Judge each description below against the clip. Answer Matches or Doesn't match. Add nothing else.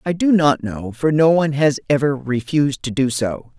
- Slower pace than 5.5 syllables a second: Matches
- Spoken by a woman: Matches